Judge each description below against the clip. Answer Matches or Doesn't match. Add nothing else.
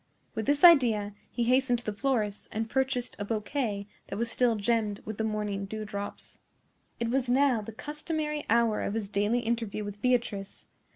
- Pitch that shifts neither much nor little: Matches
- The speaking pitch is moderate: Doesn't match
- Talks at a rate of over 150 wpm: Matches